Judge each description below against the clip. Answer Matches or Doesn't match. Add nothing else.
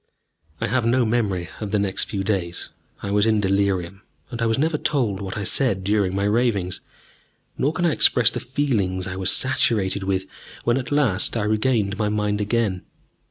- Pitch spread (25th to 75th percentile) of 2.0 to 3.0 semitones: Doesn't match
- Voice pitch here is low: Matches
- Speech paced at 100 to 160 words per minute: Doesn't match